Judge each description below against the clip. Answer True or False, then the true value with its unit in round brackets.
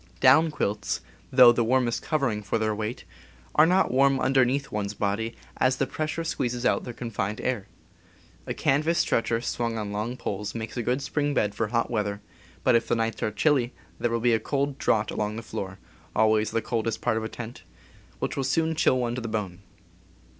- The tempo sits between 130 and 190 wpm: False (200 wpm)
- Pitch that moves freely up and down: False (3.5 semitones)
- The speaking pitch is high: False (120 Hz)